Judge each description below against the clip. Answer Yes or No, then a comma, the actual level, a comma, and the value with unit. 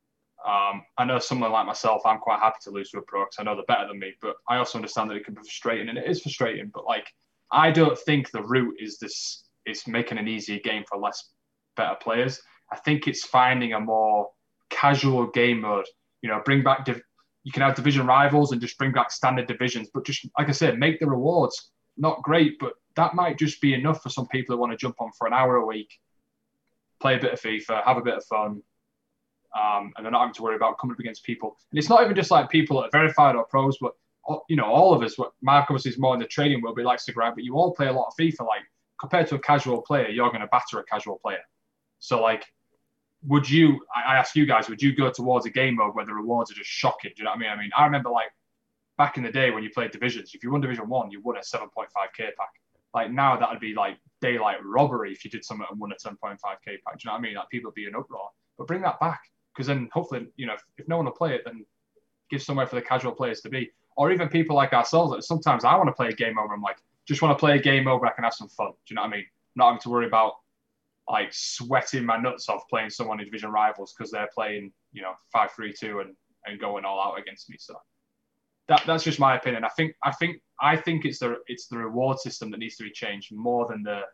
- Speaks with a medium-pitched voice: No, low, 125 Hz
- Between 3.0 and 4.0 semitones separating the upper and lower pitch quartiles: No, average, 4.5 semitones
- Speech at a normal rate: No, fast, 265 wpm